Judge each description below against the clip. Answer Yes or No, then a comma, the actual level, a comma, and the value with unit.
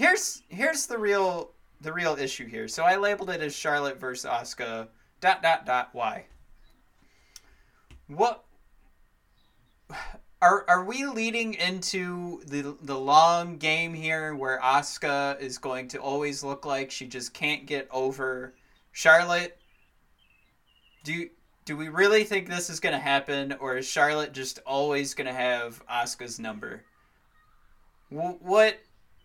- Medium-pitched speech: Yes, medium, 150 Hz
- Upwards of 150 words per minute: No, slow, 135 wpm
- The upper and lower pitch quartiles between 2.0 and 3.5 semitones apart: No, average, 5.1 semitones